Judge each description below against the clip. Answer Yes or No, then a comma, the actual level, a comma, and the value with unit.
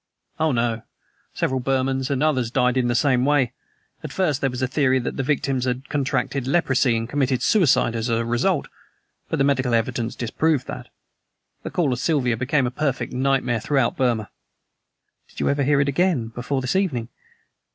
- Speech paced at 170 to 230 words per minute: Yes, average, 185 wpm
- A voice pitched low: Yes, low, 130 Hz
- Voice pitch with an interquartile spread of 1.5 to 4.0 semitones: Yes, narrow, 2.6 semitones